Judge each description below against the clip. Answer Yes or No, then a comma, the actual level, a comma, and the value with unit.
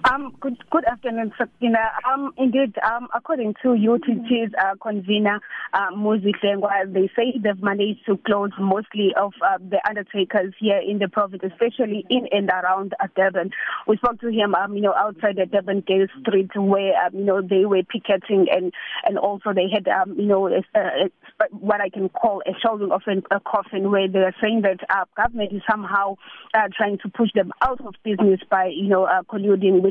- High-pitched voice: Yes, high, 205 Hz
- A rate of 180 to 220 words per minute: Yes, average, 195 wpm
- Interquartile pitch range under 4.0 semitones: Yes, narrow, 2.5 semitones